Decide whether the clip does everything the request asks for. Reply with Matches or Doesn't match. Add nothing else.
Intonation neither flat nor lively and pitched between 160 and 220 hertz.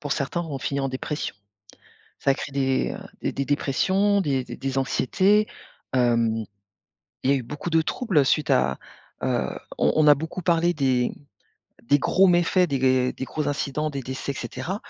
Doesn't match